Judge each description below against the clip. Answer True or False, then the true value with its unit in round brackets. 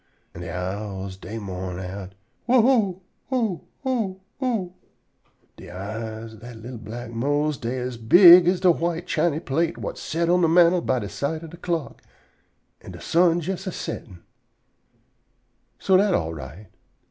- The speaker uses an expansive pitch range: True (8.7 semitones)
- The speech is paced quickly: False (160 wpm)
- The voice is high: False (145 Hz)